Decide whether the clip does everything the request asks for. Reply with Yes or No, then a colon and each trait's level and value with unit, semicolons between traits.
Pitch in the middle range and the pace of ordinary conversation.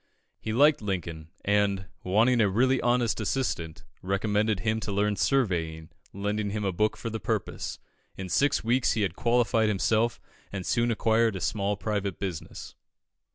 No: low, 105 Hz; average, 155 wpm